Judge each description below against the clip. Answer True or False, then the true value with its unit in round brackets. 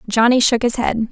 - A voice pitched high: True (235 Hz)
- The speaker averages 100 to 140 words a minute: False (215 wpm)